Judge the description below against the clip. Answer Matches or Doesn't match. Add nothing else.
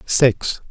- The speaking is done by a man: Matches